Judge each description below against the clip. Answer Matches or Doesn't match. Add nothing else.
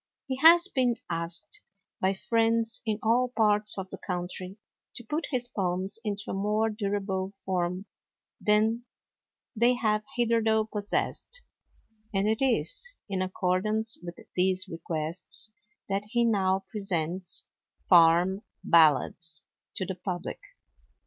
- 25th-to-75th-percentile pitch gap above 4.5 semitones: Doesn't match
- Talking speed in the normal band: Doesn't match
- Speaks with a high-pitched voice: Matches